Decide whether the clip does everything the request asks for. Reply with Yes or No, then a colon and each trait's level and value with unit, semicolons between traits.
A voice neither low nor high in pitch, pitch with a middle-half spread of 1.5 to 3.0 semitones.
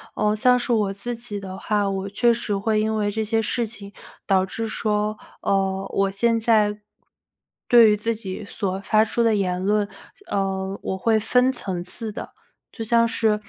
No: high, 210 Hz; narrow, 2.5 semitones